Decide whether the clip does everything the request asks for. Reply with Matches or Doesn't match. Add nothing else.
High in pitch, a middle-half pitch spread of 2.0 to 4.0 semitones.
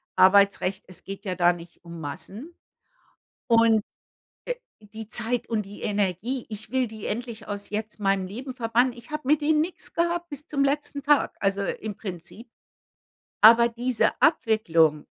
Doesn't match